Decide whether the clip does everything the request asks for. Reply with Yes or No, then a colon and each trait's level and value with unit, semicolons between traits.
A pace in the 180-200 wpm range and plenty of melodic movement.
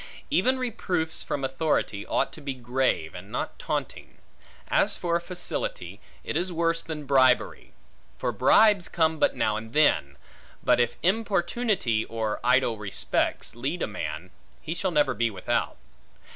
No: average, 145 wpm; wide, 7.1 semitones